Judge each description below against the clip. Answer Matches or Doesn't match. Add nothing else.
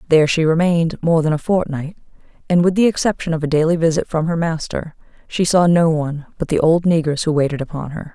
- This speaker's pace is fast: Matches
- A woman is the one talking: Matches